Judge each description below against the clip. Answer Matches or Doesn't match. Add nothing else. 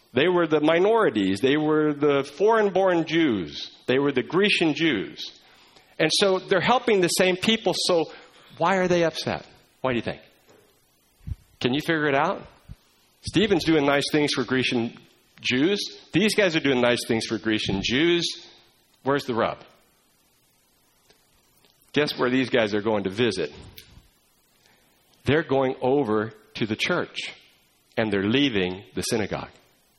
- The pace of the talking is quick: Doesn't match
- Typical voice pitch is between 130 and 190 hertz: Matches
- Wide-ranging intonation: Matches